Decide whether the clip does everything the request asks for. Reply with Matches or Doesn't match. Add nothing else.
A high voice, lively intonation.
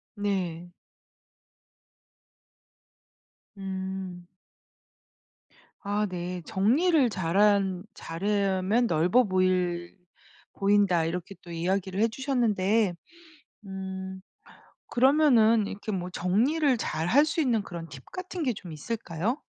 Doesn't match